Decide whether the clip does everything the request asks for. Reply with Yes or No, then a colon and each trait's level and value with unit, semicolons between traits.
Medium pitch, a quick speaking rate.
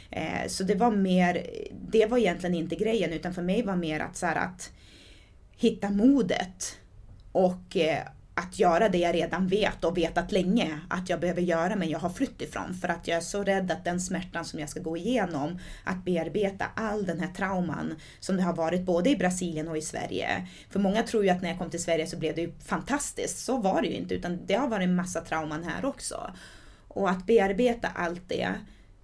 Yes: medium, 175 Hz; fast, 215 wpm